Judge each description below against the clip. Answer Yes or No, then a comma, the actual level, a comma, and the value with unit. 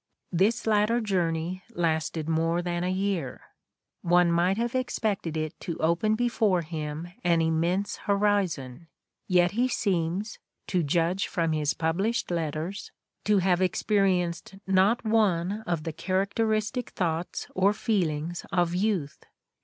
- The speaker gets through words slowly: Yes, slow, 130 wpm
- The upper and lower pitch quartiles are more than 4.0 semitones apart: No, average, 3.7 semitones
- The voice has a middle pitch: Yes, medium, 180 Hz